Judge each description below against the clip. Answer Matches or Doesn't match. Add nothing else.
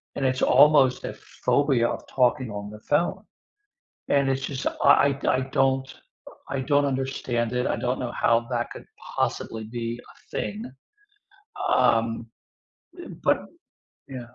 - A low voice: Matches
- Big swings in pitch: Doesn't match